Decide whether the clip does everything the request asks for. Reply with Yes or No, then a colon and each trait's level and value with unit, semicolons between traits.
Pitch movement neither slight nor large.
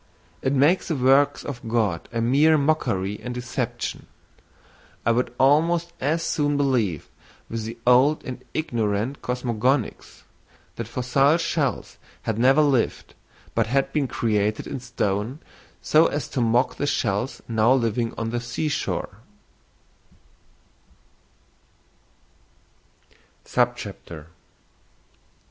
Yes: average, 3.9 semitones